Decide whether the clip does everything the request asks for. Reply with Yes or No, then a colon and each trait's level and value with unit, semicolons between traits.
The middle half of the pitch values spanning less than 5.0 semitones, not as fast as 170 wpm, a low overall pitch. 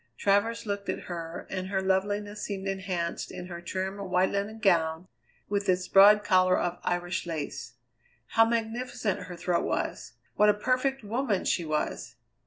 No: average, 2.7 semitones; average, 160 wpm; high, 195 Hz